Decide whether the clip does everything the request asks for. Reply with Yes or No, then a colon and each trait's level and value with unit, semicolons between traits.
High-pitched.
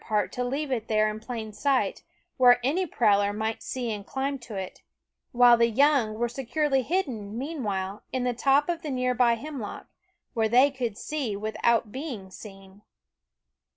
Yes: high, 240 Hz